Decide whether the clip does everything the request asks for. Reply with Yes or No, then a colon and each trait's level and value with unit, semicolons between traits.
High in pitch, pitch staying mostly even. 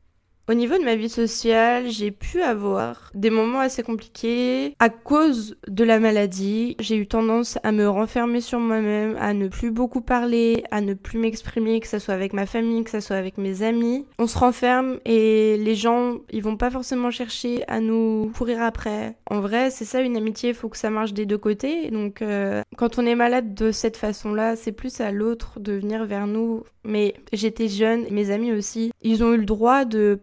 Yes: high, 225 Hz; narrow, 2.0 semitones